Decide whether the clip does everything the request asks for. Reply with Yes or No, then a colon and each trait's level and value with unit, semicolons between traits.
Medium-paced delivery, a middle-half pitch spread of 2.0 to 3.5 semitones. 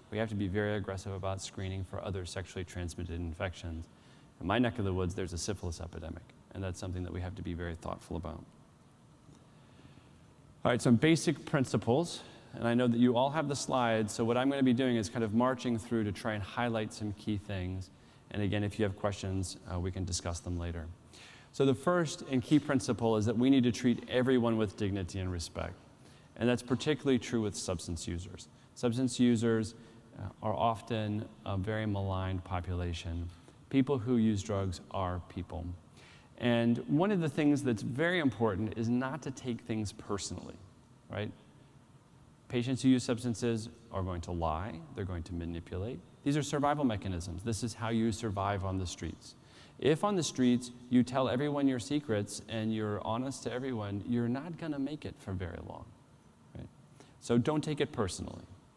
No: average, 190 wpm; average, 5.0 semitones